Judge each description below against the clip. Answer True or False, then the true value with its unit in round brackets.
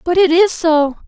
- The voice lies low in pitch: False (335 Hz)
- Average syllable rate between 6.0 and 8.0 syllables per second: False (4.4 syllables/s)